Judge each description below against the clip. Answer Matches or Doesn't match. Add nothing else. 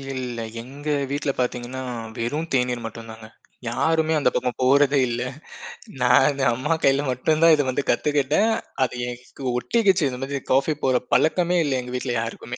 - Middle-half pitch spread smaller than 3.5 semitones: Matches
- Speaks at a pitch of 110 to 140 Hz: Matches